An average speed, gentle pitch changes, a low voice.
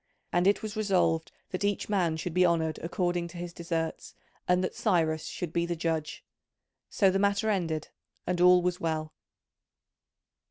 No: average, 165 wpm; narrow, 2.3 semitones; medium, 175 Hz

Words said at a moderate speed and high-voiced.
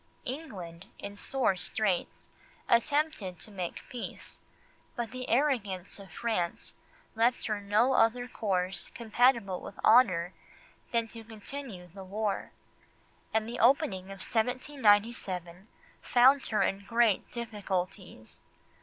No: slow, 115 wpm; high, 220 Hz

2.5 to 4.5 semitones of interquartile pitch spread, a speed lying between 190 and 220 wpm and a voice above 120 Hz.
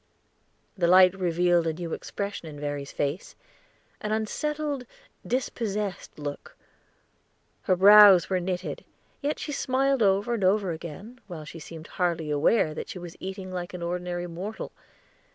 No: average, 3.8 semitones; average, 145 wpm; medium, 185 Hz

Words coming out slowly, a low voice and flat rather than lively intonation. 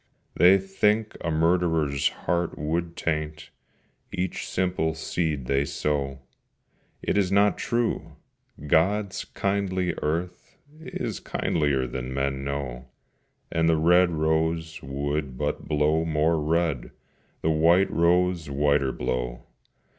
No: slow, 115 wpm; very low, 80 Hz; average, 3.6 semitones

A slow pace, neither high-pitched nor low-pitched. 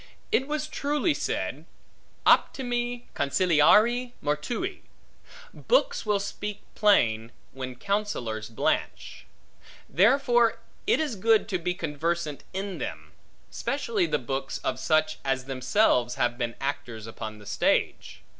Yes: slow, 115 wpm; medium, 180 Hz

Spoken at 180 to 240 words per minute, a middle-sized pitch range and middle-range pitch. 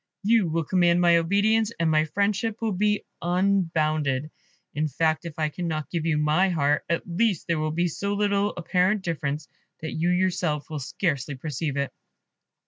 No: average, 170 wpm; average, 3.9 semitones; medium, 170 Hz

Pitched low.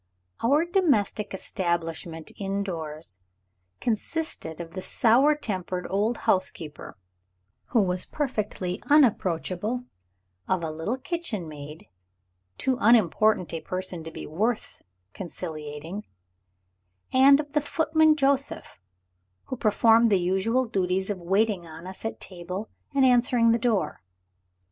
No: high, 200 Hz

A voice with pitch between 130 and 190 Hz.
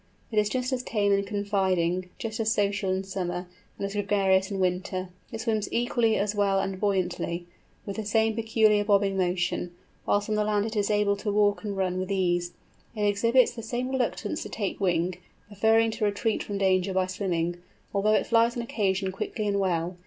No: high, 200 Hz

